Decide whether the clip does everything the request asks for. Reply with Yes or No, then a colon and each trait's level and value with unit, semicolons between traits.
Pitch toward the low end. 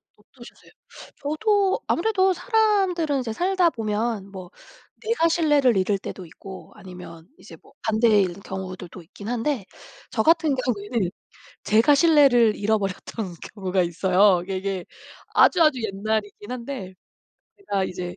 No: high, 220 Hz